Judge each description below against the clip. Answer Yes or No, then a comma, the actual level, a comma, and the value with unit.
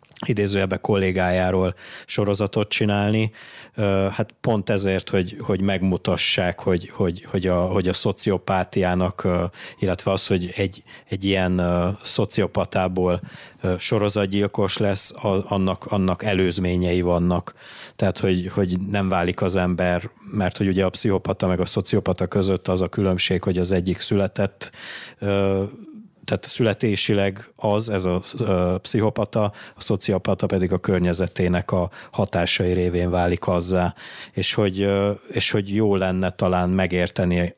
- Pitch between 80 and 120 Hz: Yes, very low, 95 Hz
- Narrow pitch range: Yes, narrow, 1.9 semitones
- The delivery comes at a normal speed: Yes, average, 125 wpm